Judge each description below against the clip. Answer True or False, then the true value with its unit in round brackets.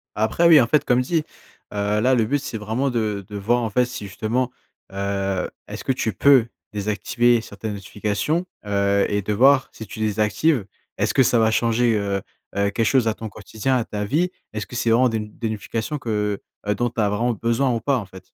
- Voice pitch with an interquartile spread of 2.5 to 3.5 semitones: True (3.2 semitones)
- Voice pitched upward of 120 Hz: False (110 Hz)